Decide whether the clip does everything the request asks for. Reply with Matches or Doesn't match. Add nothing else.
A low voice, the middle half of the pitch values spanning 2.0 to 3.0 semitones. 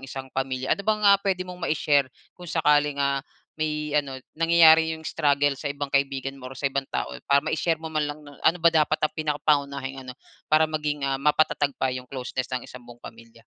Doesn't match